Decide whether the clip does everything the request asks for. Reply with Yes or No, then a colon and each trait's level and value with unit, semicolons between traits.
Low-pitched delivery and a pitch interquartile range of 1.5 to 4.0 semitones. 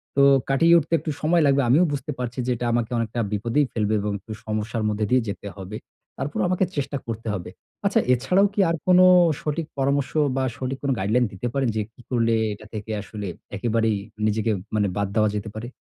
No: low, 120 Hz; average, 4.5 semitones